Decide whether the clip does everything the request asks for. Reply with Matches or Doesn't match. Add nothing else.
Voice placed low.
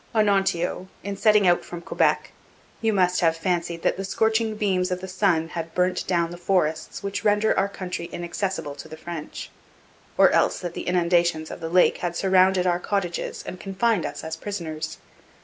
Doesn't match